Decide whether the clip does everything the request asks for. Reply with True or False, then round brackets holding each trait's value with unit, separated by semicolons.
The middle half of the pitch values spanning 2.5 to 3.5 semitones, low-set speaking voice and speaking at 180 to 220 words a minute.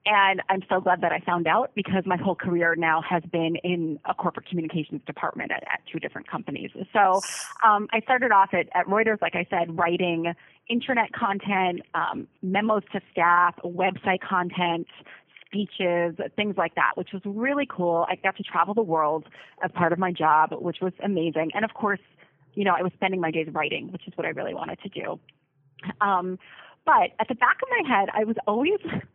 False (3.2 semitones; 185 Hz; 200 wpm)